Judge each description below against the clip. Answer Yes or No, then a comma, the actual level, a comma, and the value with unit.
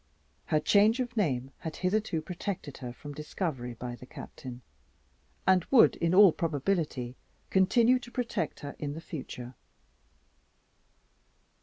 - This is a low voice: No, medium, 160 Hz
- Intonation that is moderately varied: No, wide, 7.1 semitones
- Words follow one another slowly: Yes, slow, 130 wpm